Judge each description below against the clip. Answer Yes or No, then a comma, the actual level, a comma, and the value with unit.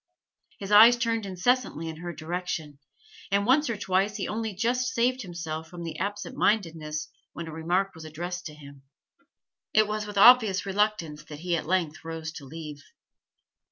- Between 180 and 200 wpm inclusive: No, average, 165 wpm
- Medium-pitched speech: Yes, medium, 180 Hz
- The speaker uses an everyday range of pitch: Yes, average, 4.8 semitones